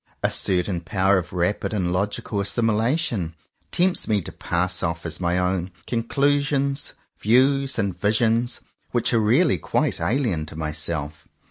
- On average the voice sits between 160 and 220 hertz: No, low, 100 Hz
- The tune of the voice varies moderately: No, wide, 5.7 semitones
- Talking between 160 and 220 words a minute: No, average, 150 wpm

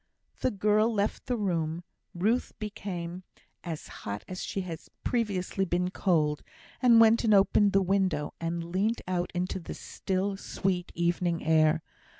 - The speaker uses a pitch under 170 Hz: No, medium, 185 Hz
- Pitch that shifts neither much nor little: Yes, average, 3.1 semitones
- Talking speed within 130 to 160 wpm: Yes, average, 150 wpm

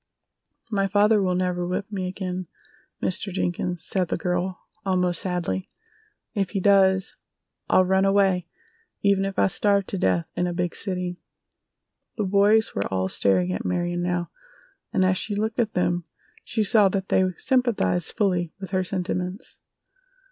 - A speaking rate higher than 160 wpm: No, average, 155 wpm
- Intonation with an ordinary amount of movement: No, narrow, 2.0 semitones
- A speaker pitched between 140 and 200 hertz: Yes, medium, 185 Hz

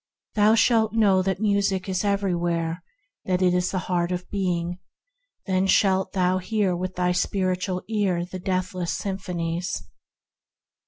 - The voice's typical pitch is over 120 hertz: Yes, medium, 185 Hz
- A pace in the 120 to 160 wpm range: Yes, average, 140 wpm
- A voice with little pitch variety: Yes, narrow, 1.6 semitones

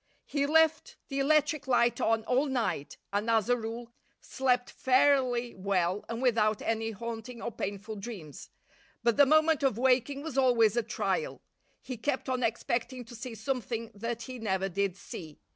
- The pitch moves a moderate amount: Yes, average, 3.1 semitones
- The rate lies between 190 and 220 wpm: No, average, 165 wpm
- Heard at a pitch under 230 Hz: No, high, 235 Hz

